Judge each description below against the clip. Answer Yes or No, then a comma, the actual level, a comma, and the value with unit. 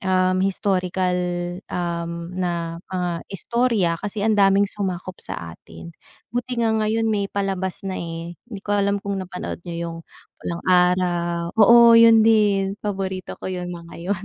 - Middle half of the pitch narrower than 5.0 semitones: Yes, average, 2.8 semitones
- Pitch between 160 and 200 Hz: Yes, high, 190 Hz